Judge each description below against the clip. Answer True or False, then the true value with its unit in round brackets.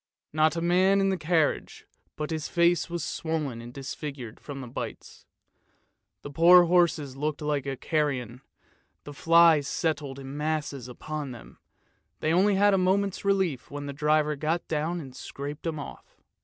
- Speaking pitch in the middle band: True (155 Hz)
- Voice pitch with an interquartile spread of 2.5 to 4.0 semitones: True (3.4 semitones)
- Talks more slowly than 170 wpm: True (160 wpm)